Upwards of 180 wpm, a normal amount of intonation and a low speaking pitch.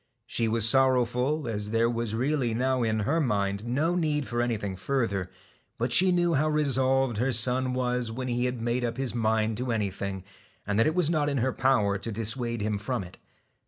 Yes: average, 200 wpm; average, 3.3 semitones; low, 120 Hz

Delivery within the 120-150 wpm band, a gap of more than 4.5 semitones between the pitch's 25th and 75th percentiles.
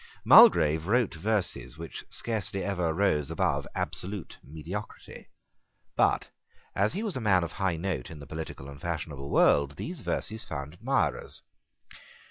Yes: average, 140 wpm; average, 5.2 semitones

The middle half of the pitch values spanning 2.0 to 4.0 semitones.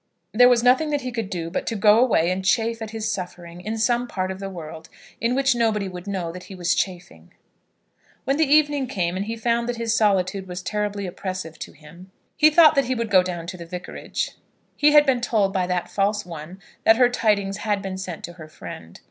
No: average, 4.5 semitones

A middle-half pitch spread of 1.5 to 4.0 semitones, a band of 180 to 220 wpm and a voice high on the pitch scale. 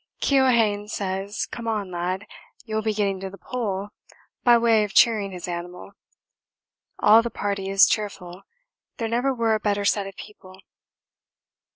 No: narrow, 2.6 semitones; average, 155 wpm; high, 205 Hz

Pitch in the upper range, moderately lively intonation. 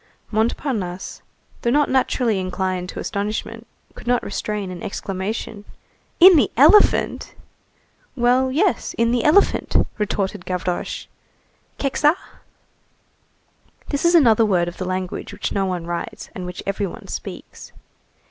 No: high, 210 Hz; wide, 5.7 semitones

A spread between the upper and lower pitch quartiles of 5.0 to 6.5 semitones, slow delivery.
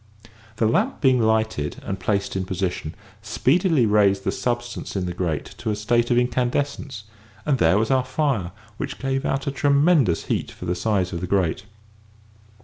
No: wide, 5.6 semitones; average, 175 wpm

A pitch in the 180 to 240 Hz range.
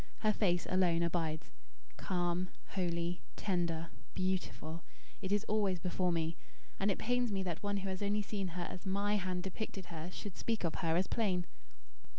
Yes: medium, 185 Hz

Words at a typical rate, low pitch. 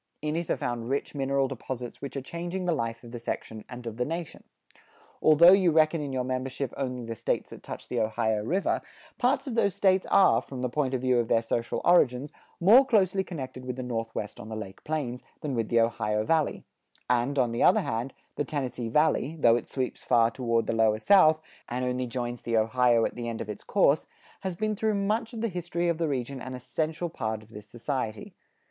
No: fast, 220 wpm; low, 130 Hz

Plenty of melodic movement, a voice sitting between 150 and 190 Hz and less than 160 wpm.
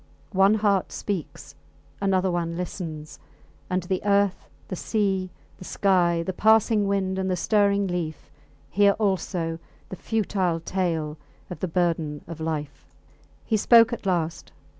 No: average, 3.1 semitones; medium, 185 Hz; average, 140 wpm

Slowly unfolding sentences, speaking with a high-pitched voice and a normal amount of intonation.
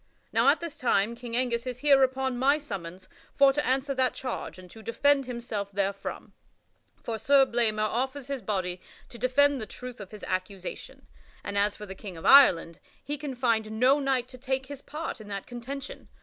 No: average, 195 wpm; high, 245 Hz; average, 4.4 semitones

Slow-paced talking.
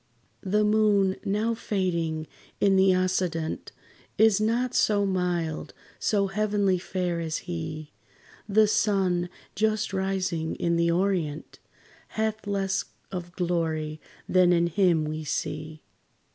Yes: slow, 115 wpm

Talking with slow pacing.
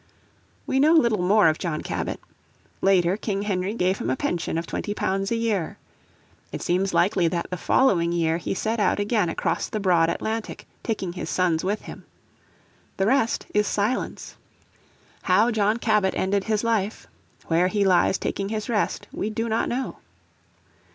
No: average, 165 wpm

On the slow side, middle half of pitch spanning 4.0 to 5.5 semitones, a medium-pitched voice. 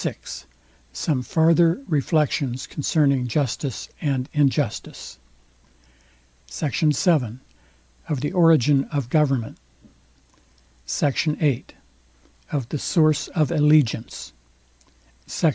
No: slow, 90 wpm; average, 3.0 semitones; medium, 145 Hz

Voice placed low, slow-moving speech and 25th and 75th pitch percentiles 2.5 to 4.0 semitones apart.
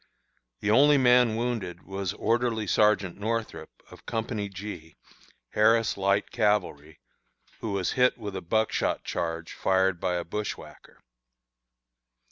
Yes: low, 105 Hz; slow, 120 wpm; average, 3.3 semitones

